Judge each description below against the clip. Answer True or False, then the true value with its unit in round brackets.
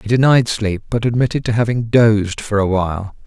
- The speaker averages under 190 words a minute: False (200 wpm)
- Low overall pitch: True (110 Hz)